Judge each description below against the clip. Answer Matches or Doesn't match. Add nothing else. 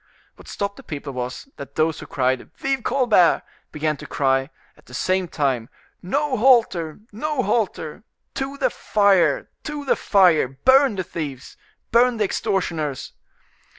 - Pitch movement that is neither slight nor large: Doesn't match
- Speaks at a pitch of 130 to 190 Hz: Matches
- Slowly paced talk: Doesn't match